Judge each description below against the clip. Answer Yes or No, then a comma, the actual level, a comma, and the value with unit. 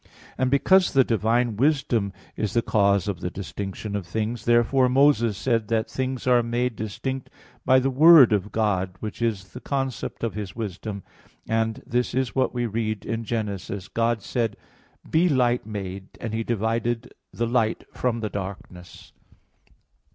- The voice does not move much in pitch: No, average, 3.3 semitones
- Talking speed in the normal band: Yes, average, 165 wpm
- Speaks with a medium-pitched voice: No, low, 115 Hz